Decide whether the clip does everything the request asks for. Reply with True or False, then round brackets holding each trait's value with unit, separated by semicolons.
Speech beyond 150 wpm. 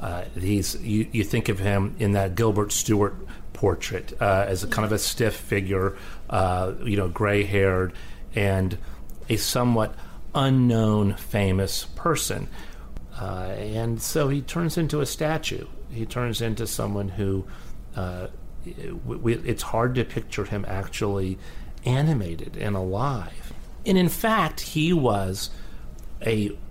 False (135 wpm)